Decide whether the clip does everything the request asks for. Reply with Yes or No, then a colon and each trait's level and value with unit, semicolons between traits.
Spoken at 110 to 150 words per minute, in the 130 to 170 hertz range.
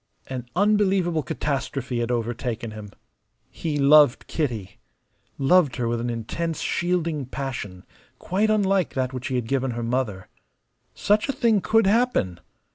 Yes: average, 140 wpm; low, 135 Hz